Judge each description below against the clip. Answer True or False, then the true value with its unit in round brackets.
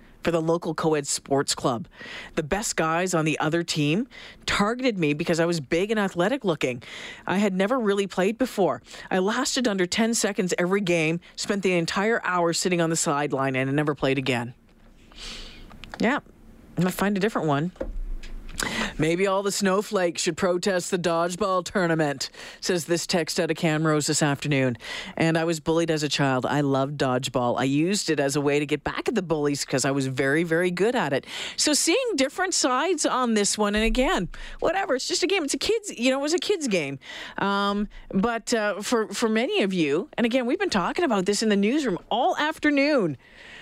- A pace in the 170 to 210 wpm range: True (200 wpm)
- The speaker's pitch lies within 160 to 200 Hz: True (185 Hz)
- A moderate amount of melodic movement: False (6.2 semitones)